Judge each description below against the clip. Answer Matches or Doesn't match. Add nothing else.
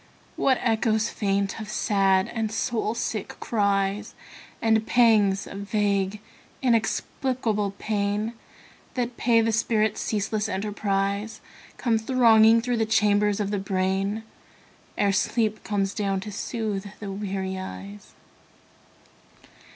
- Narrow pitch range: Matches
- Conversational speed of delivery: Doesn't match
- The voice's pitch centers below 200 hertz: Doesn't match